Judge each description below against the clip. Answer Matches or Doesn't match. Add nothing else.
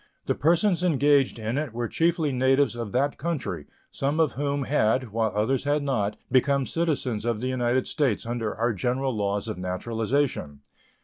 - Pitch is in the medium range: Doesn't match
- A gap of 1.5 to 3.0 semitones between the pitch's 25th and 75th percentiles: Doesn't match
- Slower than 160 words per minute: Doesn't match